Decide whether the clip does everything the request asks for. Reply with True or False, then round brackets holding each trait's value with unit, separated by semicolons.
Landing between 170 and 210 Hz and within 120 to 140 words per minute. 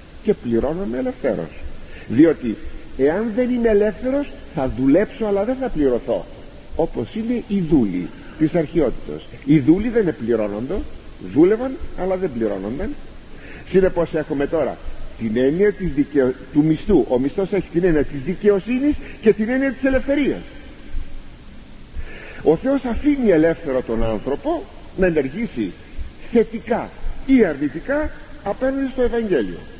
True (190 Hz; 125 wpm)